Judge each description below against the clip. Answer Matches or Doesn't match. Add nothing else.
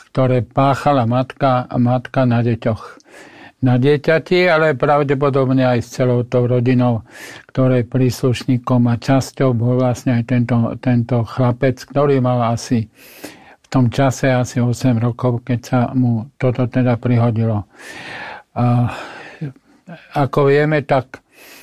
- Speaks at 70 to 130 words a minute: Matches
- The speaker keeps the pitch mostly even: Matches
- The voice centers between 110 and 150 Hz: Matches